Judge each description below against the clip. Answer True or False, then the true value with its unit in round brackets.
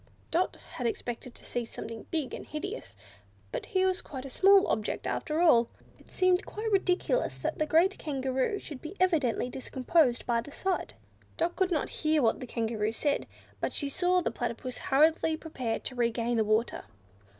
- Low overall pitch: False (285 Hz)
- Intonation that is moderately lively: False (6.7 semitones)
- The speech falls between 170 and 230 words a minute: True (180 wpm)